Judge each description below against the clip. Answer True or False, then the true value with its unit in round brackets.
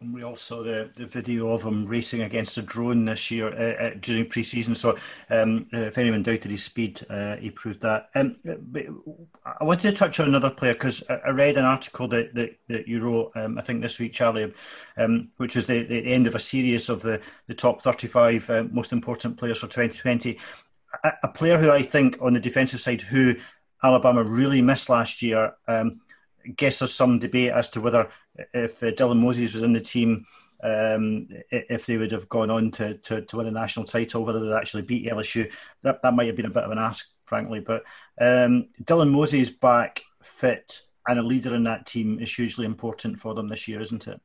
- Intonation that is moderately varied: False (1.6 semitones)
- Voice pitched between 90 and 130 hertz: True (115 Hz)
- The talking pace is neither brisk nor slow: False (215 wpm)